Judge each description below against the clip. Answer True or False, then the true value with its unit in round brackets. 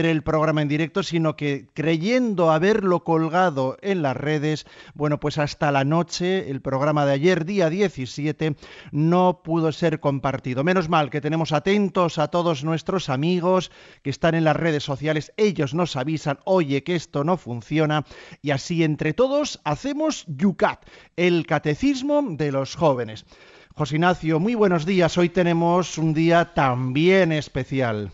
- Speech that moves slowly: False (155 wpm)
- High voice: False (160 Hz)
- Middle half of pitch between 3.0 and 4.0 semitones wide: True (3.3 semitones)